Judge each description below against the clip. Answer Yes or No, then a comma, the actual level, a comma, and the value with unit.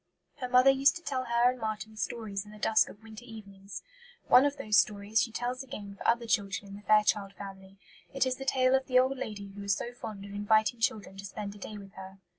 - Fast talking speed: Yes, fast, 240 wpm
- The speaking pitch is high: Yes, high, 215 Hz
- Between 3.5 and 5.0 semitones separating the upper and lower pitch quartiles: Yes, average, 3.8 semitones